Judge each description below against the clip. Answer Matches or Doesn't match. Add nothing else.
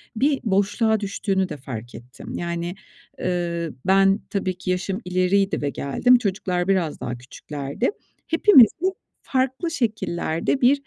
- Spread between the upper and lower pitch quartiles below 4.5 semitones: Doesn't match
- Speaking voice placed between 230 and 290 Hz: Doesn't match